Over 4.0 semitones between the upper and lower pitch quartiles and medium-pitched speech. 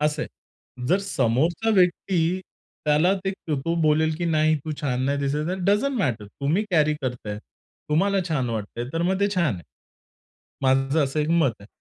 Yes: average, 4.5 semitones; medium, 155 Hz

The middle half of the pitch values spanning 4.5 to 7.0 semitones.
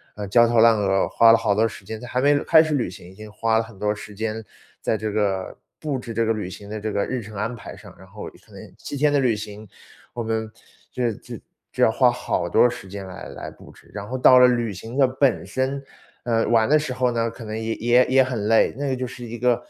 No: average, 3.0 semitones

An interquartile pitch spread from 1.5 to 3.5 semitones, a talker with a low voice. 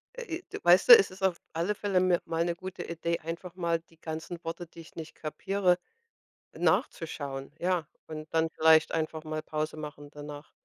No: narrow, 2.5 semitones; medium, 165 Hz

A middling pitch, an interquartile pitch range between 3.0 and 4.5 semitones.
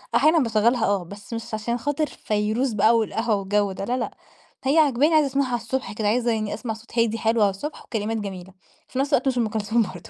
No: high, 225 Hz; average, 3.4 semitones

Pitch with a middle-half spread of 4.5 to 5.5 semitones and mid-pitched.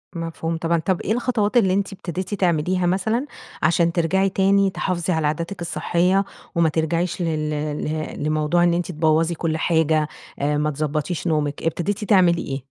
No: average, 2.9 semitones; medium, 170 Hz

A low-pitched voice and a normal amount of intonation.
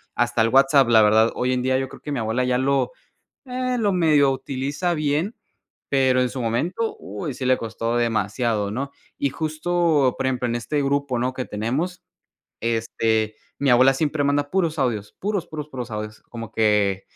Yes: low, 130 Hz; average, 4.2 semitones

